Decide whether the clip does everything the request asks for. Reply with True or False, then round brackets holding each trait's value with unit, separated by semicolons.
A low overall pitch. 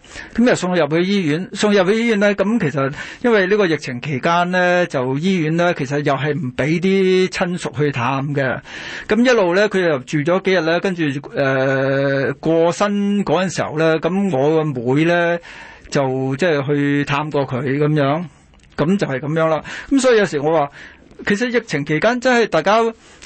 False (160 Hz)